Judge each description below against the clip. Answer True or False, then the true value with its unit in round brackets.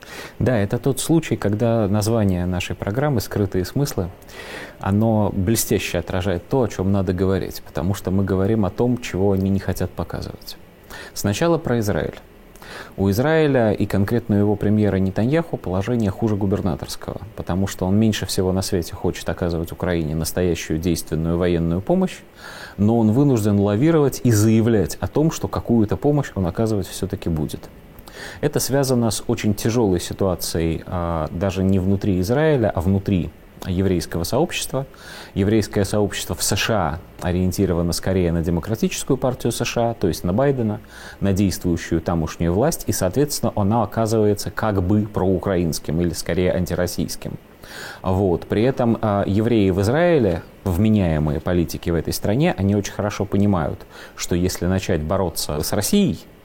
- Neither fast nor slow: True (145 wpm)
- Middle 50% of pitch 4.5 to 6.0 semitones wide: False (3.9 semitones)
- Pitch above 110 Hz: False (100 Hz)